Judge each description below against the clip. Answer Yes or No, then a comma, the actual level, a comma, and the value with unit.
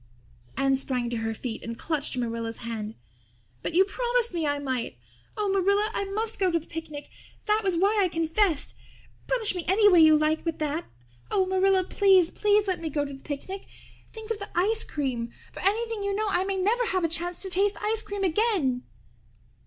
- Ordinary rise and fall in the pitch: No, wide, 5.8 semitones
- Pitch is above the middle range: Yes, very high, 365 Hz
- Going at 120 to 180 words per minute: No, average, 200 wpm